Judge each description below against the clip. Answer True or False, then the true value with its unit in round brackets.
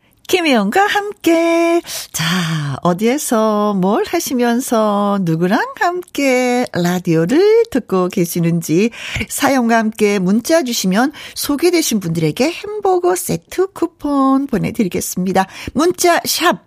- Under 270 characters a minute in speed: True (240 characters per minute)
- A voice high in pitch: True (245 Hz)